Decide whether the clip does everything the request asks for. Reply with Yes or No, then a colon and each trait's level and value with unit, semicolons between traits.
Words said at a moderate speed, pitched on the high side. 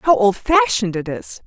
Yes: average, 165 wpm; high, 235 Hz